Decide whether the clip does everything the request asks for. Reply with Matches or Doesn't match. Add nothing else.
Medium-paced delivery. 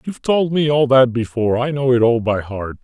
Doesn't match